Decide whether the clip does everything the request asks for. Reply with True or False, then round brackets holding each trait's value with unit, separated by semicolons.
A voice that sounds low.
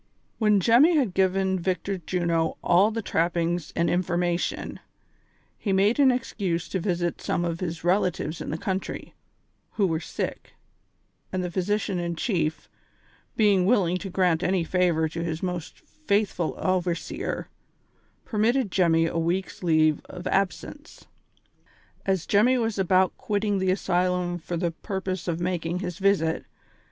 False (180 Hz)